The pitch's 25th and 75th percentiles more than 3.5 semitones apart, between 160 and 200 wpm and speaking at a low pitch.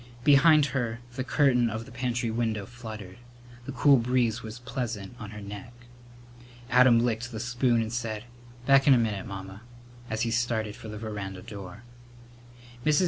No: narrow, 2.6 semitones; average, 165 wpm; low, 115 Hz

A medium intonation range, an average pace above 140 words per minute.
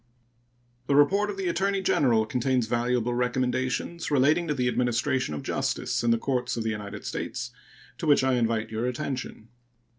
Yes: average, 3.5 semitones; average, 170 wpm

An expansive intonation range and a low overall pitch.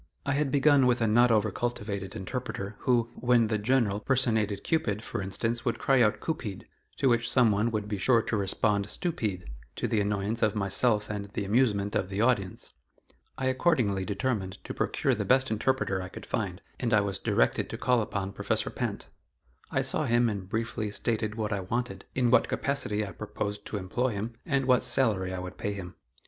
No: average, 3.5 semitones; low, 110 Hz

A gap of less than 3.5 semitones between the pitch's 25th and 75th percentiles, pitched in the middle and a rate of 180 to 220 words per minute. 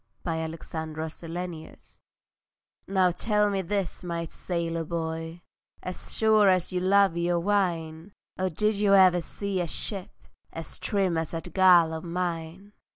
No: average, 2.9 semitones; medium, 175 Hz; average, 155 wpm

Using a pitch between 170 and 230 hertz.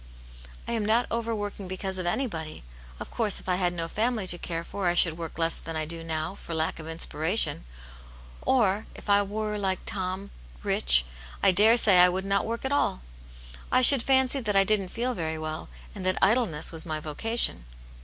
Yes: high, 190 Hz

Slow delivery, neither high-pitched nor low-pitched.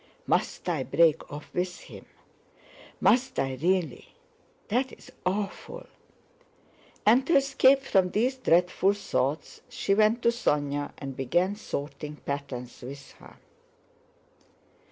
Yes: slow, 115 wpm; medium, 180 Hz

